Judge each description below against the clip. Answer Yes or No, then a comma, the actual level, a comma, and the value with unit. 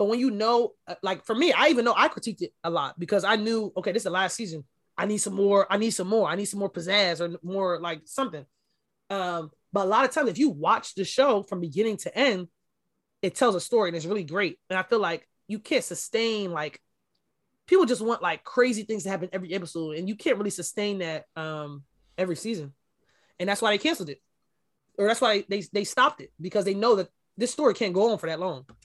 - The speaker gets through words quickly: Yes, fast, 240 wpm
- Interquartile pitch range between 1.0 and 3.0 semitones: No, average, 4.0 semitones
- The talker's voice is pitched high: Yes, high, 200 Hz